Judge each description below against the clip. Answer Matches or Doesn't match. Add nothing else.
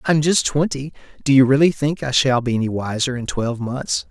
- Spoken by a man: Matches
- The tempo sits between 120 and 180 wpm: Doesn't match